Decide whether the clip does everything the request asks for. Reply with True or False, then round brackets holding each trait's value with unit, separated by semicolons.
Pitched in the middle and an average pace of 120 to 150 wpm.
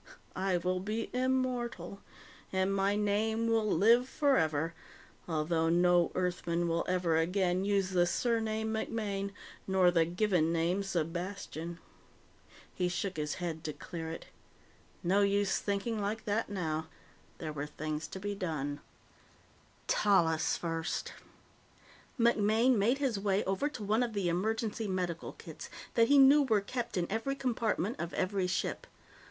False (195 Hz; 140 wpm)